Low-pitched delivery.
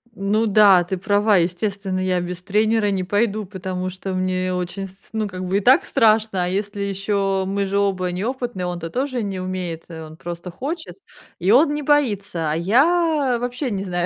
No: high, 195 Hz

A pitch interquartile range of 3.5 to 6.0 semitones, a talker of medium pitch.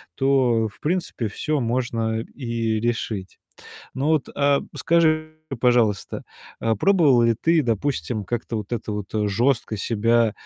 No: average, 4.0 semitones; low, 120 Hz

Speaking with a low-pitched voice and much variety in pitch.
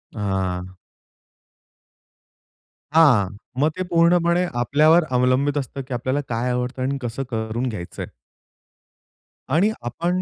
Yes: low, 130 Hz; wide, 5.7 semitones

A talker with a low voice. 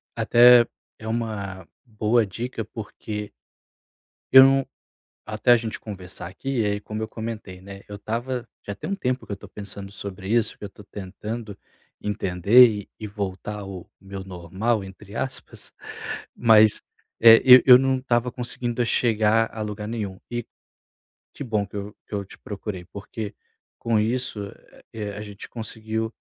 Yes: low, 110 Hz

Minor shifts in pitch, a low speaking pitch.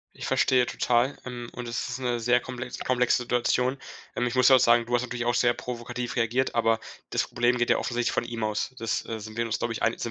Yes: narrow, 1.0 semitones; low, 120 Hz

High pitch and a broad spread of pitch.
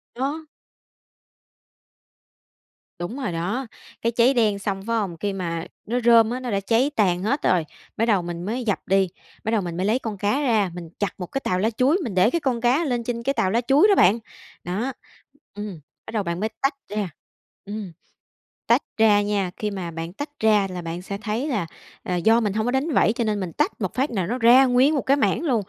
No: high, 215 Hz; average, 4.5 semitones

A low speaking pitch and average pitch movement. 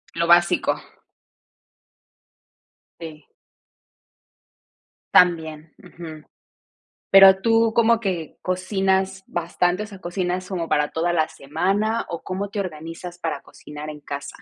No: medium, 175 Hz; average, 3.1 semitones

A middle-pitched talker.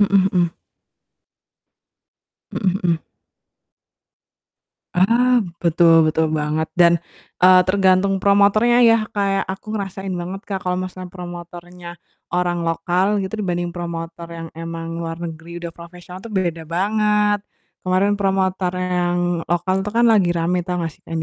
Yes: medium, 180 Hz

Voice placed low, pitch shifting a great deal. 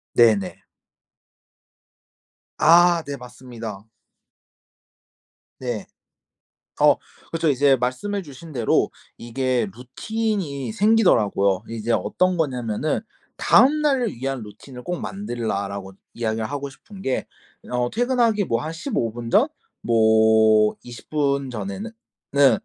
Yes: low, 130 Hz; wide, 7.3 semitones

